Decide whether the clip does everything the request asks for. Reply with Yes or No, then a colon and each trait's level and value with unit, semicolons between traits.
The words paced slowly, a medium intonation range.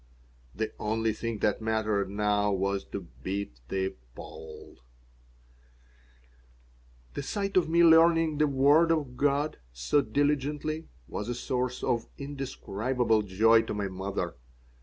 No: slow, 125 wpm; wide, 6.1 semitones